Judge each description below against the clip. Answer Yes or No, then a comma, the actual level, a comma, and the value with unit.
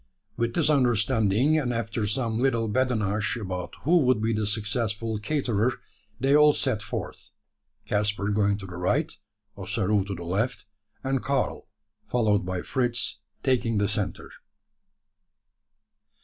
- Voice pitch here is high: No, low, 110 Hz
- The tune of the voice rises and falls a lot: No, average, 3.7 semitones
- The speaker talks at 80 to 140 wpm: Yes, slow, 135 wpm